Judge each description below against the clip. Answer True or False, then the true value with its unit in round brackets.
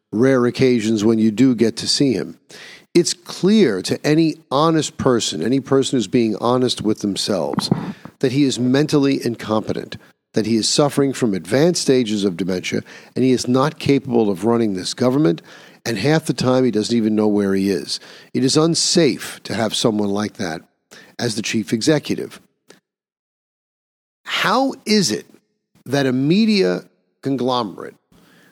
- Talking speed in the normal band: True (160 wpm)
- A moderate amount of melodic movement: True (5.0 semitones)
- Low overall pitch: True (125 Hz)